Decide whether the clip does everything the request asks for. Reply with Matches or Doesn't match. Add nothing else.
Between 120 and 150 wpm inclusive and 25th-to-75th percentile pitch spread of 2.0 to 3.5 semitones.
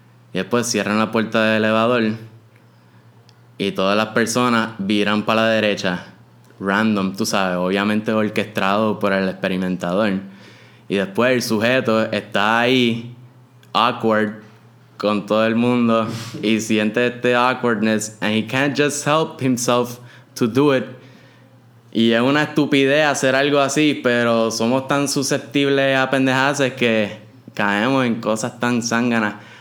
Matches